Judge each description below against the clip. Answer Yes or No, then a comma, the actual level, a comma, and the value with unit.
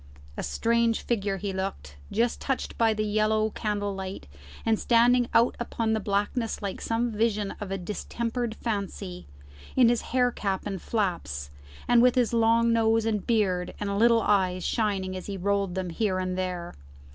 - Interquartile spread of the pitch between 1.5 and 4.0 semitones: Yes, average, 3.3 semitones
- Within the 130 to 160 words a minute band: No, average, 170 wpm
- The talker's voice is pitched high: Yes, high, 210 Hz